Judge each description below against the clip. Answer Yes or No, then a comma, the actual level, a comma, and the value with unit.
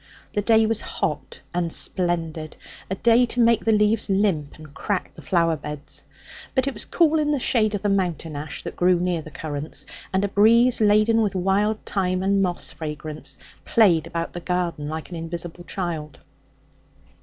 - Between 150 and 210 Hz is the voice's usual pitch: Yes, medium, 185 Hz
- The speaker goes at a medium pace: Yes, average, 180 wpm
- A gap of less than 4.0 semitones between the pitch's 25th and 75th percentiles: No, average, 4.7 semitones